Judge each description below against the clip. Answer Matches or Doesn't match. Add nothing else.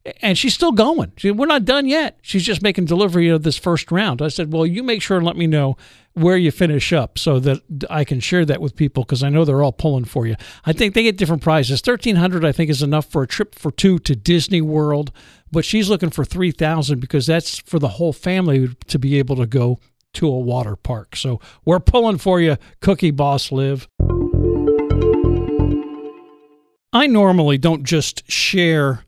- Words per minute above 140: Matches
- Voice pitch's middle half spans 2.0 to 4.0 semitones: Doesn't match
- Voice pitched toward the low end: Doesn't match